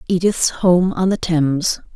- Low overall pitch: No, medium, 175 Hz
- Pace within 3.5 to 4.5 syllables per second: Yes, 4.2 syllables/s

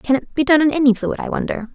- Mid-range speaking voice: No, very high, 275 Hz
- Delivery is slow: No, fast, 310 wpm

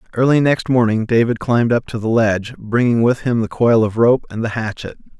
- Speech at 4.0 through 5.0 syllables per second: No, 5.6 syllables/s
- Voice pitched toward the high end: No, low, 115 Hz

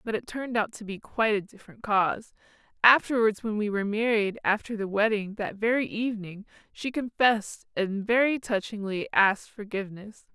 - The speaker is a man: No, female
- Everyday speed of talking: Yes, average, 160 wpm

